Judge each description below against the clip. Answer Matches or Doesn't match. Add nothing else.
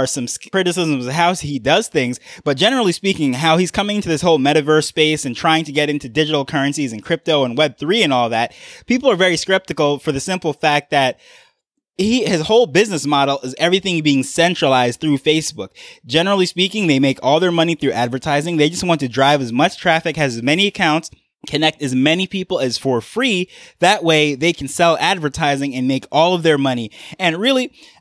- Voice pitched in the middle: Matches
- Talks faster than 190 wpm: Matches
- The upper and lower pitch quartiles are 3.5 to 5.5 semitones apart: Matches